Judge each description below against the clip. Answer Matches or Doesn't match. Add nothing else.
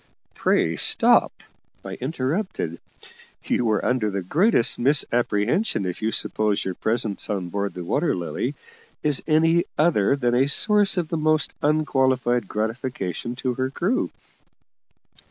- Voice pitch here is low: Matches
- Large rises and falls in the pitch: Matches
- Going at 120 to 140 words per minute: Matches